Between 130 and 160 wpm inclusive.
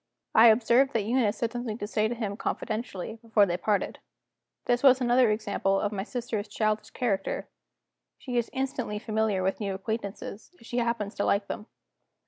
No: average, 175 wpm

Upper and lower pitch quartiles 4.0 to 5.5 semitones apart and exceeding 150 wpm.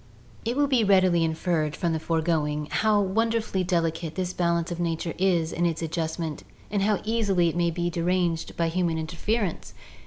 No: average, 2.7 semitones; average, 175 wpm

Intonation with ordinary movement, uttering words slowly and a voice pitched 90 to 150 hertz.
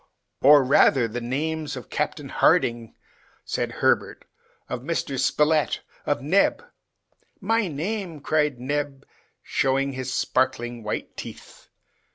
Yes: average, 3.4 semitones; slow, 120 wpm; medium, 140 Hz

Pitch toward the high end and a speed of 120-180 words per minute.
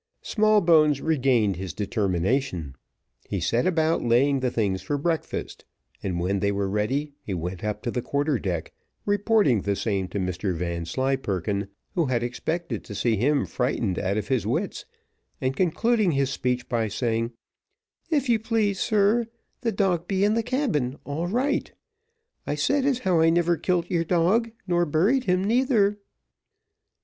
No: medium, 140 Hz; average, 160 wpm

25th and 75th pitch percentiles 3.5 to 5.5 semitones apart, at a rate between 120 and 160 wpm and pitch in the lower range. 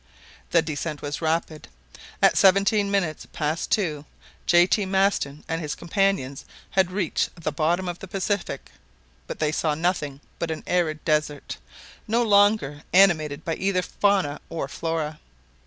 No: average, 4.1 semitones; average, 145 wpm; medium, 165 Hz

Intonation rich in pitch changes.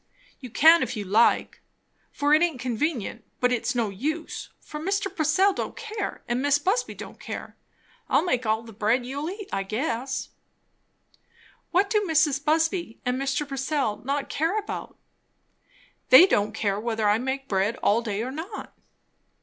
Yes: wide, 5.9 semitones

